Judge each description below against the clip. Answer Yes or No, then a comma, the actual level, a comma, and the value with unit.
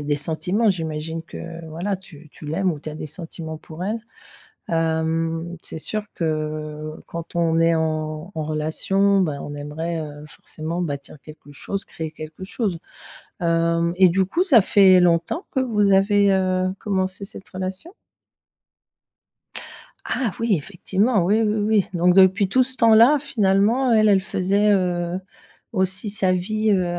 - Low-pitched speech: No, medium, 180 Hz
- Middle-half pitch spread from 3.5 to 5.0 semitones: Yes, average, 3.9 semitones